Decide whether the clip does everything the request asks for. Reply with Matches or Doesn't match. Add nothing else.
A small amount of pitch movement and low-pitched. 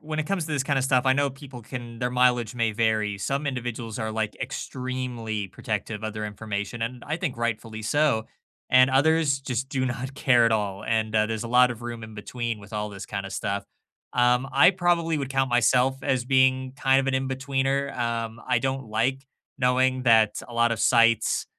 Doesn't match